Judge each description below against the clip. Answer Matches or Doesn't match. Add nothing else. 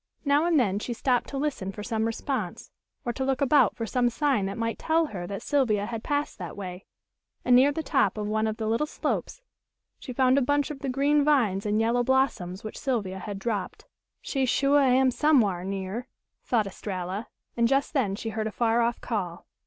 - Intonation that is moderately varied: Matches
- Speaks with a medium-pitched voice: Doesn't match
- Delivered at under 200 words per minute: Doesn't match